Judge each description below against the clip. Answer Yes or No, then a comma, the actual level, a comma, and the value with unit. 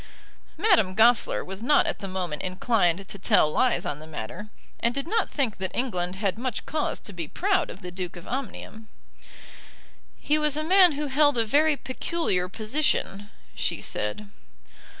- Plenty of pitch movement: Yes, wide, 7.9 semitones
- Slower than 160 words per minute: No, average, 170 wpm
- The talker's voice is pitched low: No, high, 220 Hz